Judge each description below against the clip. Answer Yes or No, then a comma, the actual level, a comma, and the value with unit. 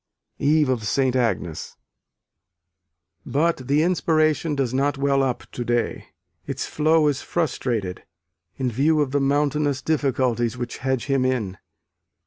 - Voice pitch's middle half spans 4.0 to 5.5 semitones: No, average, 3.2 semitones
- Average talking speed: No, slow, 130 wpm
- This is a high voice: No, low, 135 Hz